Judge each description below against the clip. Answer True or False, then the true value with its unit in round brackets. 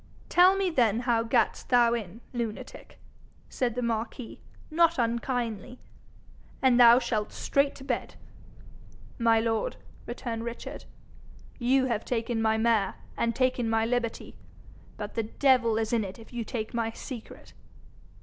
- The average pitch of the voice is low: False (235 Hz)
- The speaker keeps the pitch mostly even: True (1.8 semitones)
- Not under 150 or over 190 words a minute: False (140 wpm)